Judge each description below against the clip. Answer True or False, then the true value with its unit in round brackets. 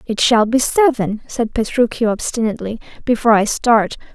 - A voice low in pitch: False (230 Hz)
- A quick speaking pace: False (145 wpm)